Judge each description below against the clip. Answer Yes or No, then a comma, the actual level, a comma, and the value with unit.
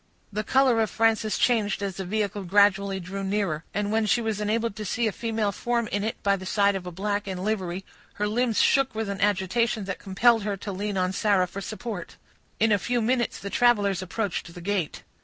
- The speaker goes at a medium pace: No, fast, 215 wpm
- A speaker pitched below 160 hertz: No, high, 205 Hz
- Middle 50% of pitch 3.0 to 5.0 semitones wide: No, narrow, 2.4 semitones